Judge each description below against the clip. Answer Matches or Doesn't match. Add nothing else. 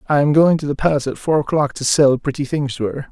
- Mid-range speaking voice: Matches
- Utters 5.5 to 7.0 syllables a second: Matches